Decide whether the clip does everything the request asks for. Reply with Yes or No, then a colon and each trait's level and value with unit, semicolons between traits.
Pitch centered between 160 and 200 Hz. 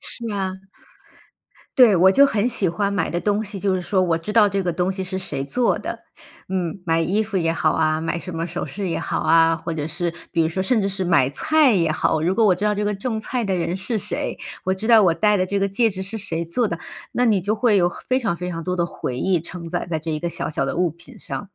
Yes: medium, 185 Hz